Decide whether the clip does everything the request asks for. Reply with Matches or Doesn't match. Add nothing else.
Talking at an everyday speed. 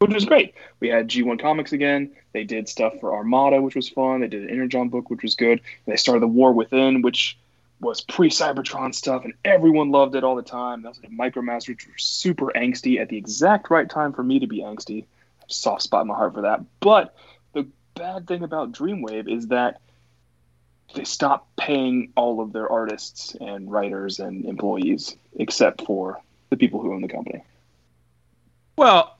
Matches